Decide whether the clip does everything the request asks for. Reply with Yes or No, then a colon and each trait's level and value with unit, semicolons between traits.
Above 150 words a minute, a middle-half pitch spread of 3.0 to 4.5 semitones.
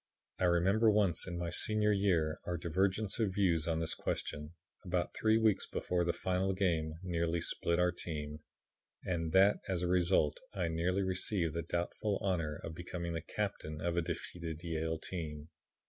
No: average, 170 wpm; narrow, 2.5 semitones